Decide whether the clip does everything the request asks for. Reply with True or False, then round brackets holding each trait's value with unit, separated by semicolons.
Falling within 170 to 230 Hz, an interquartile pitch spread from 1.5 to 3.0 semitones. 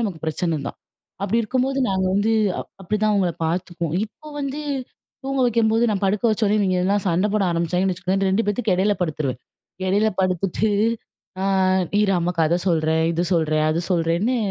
False (190 Hz; 3.9 semitones)